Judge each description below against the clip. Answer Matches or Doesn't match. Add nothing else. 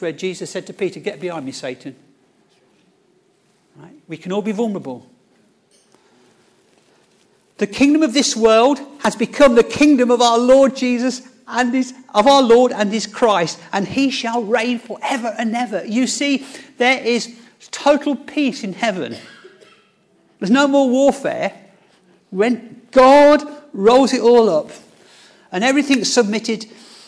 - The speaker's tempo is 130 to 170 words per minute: Matches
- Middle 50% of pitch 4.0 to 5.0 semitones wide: Matches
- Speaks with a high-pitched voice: Matches